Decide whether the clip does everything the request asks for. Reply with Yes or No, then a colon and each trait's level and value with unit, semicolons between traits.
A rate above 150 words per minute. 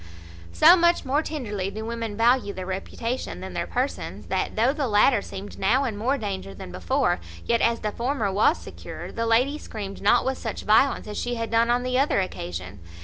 Yes: fast, 205 wpm